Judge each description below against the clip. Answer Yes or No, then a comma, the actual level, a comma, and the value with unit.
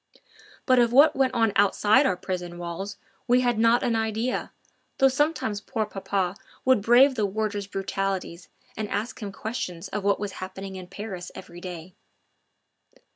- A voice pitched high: Yes, high, 205 Hz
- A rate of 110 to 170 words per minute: Yes, average, 160 wpm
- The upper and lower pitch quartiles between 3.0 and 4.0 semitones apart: Yes, average, 3.7 semitones